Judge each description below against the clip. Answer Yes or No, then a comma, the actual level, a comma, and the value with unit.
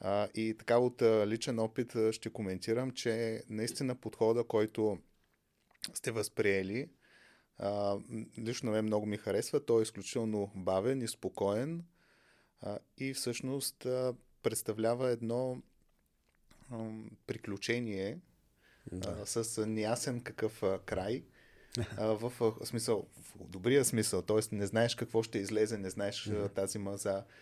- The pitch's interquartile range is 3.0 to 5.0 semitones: No, narrow, 2.5 semitones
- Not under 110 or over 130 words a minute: Yes, average, 125 wpm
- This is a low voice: Yes, low, 110 Hz